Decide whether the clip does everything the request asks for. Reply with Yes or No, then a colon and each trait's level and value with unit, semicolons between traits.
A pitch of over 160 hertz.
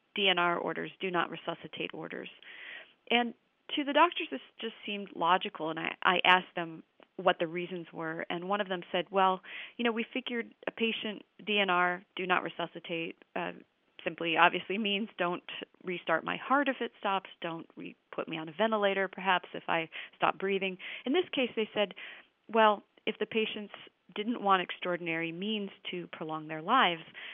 Yes: high, 190 Hz